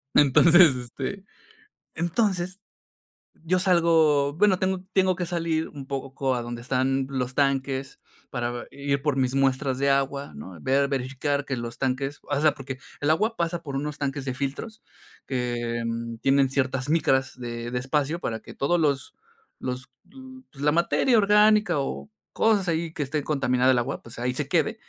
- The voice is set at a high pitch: No, medium, 140 Hz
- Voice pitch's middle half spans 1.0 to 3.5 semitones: No, average, 4.2 semitones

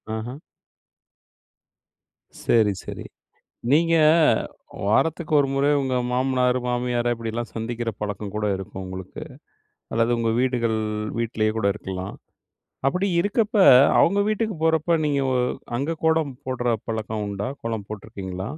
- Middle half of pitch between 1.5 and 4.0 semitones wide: No, average, 4.7 semitones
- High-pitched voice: No, low, 120 Hz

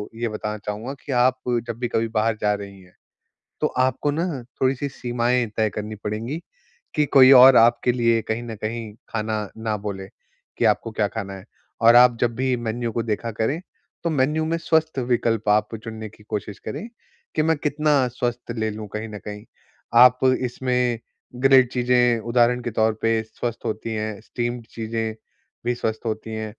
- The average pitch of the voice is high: No, low, 115 Hz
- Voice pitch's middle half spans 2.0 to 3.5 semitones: Yes, narrow, 2.5 semitones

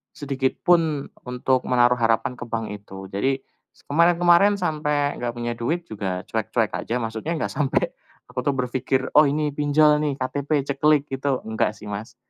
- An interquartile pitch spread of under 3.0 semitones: No, average, 4.2 semitones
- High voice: No, low, 135 Hz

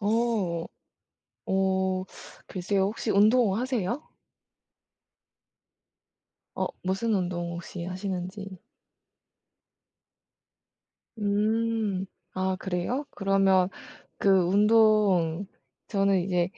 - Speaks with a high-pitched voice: Yes, high, 195 Hz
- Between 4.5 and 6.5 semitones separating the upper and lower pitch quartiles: No, narrow, 2.4 semitones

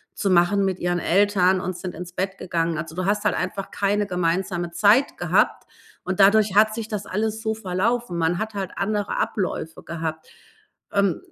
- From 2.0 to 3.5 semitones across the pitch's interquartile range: Yes, average, 2.8 semitones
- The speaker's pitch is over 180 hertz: Yes, high, 190 Hz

